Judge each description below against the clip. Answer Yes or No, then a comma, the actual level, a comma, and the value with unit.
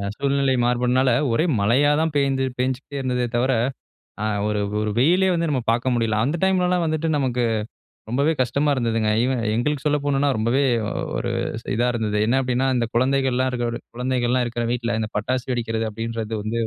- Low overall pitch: Yes, low, 125 Hz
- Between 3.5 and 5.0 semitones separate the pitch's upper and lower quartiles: No, average, 2.9 semitones